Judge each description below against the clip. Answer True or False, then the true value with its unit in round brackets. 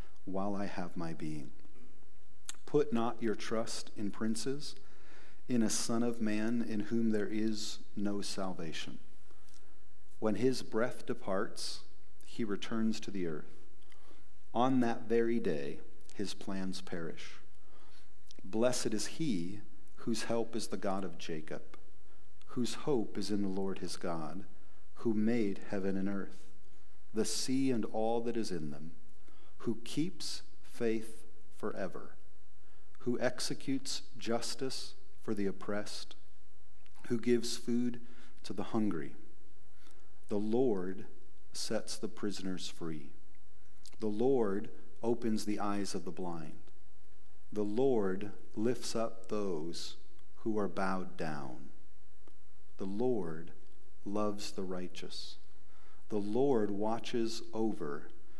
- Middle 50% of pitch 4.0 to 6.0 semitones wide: False (3.0 semitones)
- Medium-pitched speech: False (105 Hz)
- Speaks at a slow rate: True (120 wpm)